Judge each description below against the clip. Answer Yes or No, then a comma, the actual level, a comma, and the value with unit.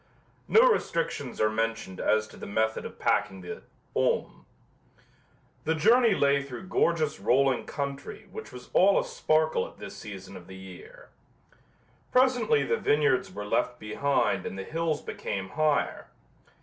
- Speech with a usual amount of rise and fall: No, wide, 8.1 semitones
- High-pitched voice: No, medium, 140 Hz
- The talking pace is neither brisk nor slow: Yes, average, 150 wpm